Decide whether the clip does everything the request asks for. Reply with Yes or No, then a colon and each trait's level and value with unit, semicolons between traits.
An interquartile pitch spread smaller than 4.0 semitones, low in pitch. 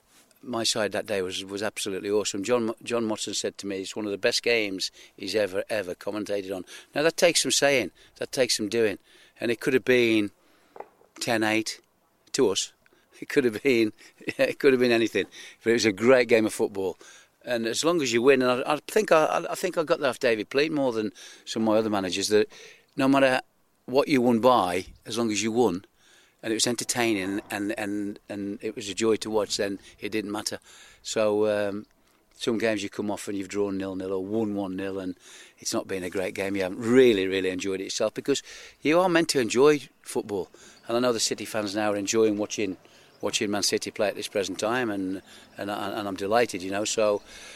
Yes: average, 3.3 semitones; low, 110 Hz